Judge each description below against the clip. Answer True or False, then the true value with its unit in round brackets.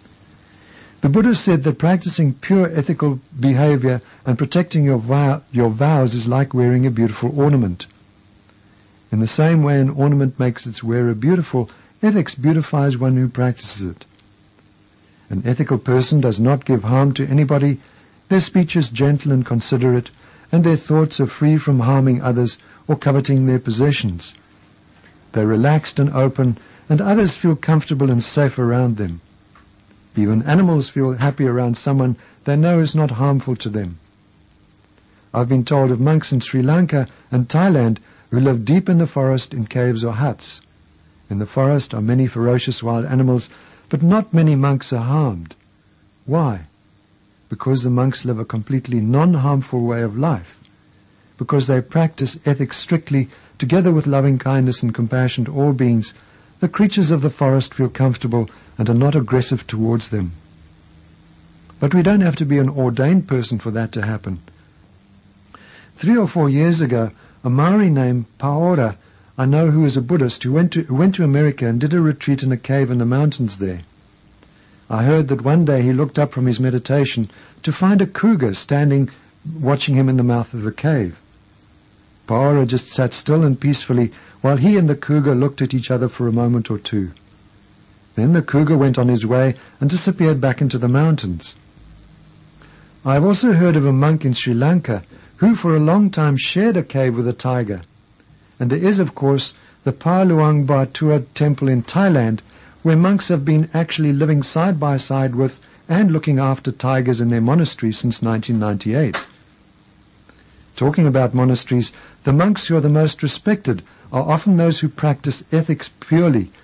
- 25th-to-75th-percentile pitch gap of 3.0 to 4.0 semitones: False (4.8 semitones)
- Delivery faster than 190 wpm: False (170 wpm)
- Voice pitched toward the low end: True (130 Hz)